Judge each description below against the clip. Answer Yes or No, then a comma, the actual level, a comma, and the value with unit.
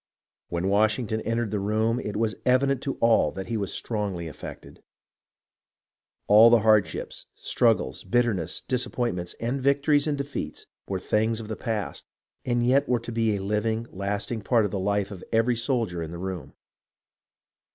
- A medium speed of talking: Yes, average, 160 wpm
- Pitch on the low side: Yes, low, 110 Hz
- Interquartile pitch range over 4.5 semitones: No, average, 3.2 semitones